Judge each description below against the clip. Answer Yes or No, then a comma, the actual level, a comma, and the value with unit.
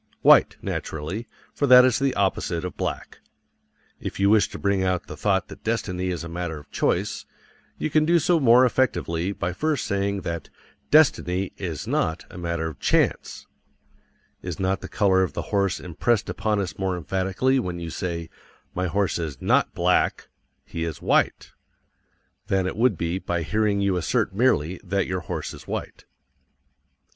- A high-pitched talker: No, very low, 95 Hz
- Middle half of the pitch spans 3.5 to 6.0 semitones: Yes, average, 3.8 semitones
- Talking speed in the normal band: Yes, average, 170 wpm